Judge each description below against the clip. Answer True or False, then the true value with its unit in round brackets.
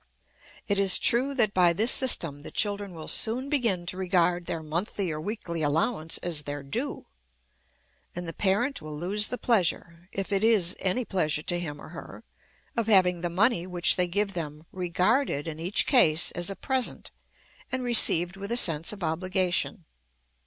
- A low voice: False (180 Hz)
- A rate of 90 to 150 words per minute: False (175 wpm)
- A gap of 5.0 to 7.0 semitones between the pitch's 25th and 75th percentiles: False (4.1 semitones)